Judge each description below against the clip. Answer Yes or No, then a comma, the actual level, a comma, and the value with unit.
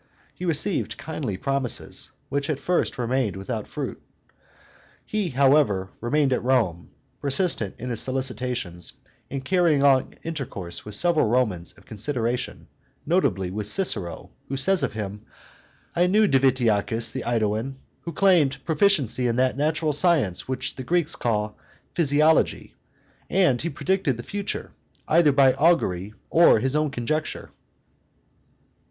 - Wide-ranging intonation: Yes, wide, 5.7 semitones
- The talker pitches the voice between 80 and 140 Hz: Yes, low, 135 Hz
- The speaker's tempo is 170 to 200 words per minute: No, slow, 135 wpm